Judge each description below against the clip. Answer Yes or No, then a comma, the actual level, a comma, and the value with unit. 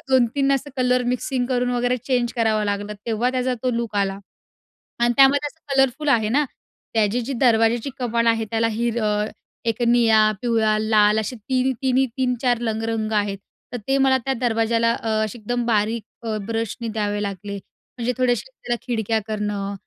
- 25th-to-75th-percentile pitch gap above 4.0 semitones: No, narrow, 2.5 semitones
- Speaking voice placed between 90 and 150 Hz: No, high, 235 Hz